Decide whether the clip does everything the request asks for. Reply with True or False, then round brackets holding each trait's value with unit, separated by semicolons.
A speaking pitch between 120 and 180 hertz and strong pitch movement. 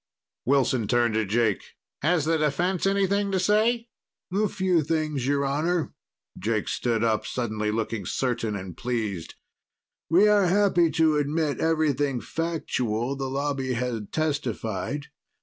True (140 Hz; 6.2 semitones)